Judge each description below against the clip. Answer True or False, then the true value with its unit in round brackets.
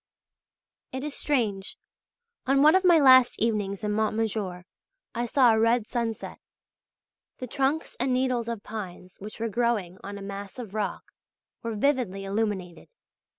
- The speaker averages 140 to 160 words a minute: True (150 wpm)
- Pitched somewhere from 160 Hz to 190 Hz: False (225 Hz)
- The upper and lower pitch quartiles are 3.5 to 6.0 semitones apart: True (4.0 semitones)